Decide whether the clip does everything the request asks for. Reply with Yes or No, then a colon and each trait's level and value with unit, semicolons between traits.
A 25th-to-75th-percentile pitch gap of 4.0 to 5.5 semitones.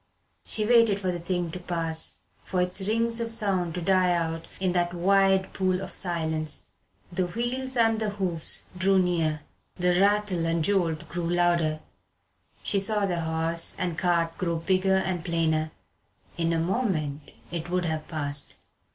No: average, 2.7 semitones